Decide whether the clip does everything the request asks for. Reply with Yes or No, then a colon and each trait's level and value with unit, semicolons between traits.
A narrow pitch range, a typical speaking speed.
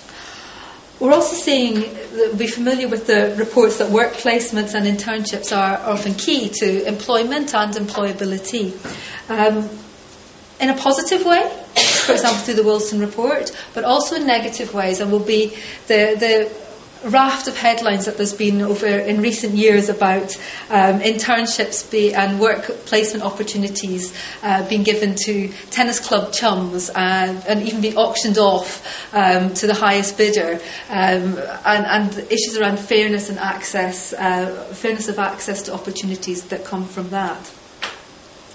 Yes: narrow, 2.2 semitones; average, 150 wpm